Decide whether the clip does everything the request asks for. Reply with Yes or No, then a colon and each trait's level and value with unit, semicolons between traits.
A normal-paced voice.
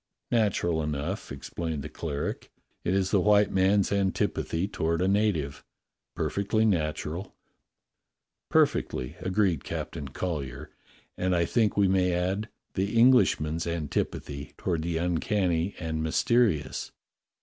No: slow, 120 wpm